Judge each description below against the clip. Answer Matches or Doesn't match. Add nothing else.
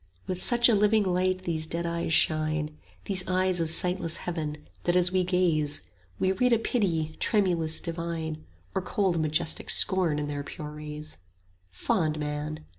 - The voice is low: Doesn't match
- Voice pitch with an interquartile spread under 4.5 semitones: Matches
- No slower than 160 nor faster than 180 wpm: Matches